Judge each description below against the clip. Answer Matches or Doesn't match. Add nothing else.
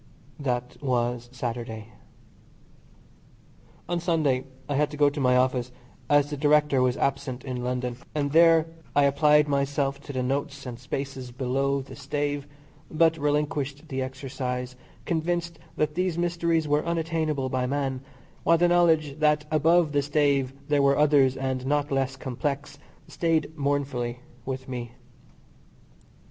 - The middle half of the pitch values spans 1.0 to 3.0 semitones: Matches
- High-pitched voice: Doesn't match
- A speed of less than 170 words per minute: Matches